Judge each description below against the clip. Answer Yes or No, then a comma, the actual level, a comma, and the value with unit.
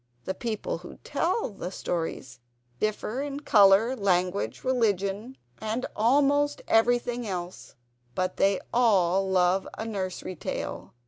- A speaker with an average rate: No, slow, 120 wpm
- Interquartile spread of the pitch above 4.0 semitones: Yes, average, 4.7 semitones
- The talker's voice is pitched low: No, high, 205 Hz